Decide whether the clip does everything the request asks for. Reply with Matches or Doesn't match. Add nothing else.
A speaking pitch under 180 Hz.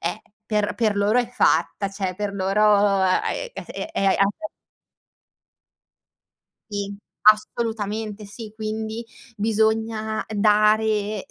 Doesn't match